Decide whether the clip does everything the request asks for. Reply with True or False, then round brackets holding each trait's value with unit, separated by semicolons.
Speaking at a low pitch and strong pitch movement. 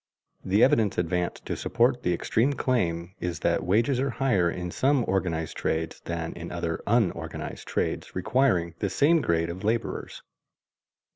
True (95 Hz; 6.4 semitones)